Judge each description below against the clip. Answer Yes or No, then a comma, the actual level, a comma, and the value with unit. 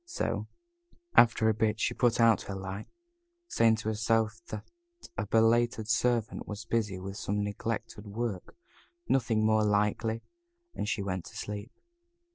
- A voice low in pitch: Yes, low, 110 Hz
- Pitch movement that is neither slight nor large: No, narrow, 1.9 semitones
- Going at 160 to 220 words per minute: No, average, 145 wpm